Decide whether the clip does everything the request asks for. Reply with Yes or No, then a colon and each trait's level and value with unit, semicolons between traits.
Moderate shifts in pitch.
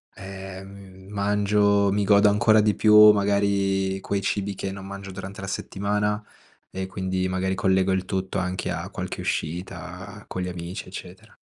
No: narrow, 1.3 semitones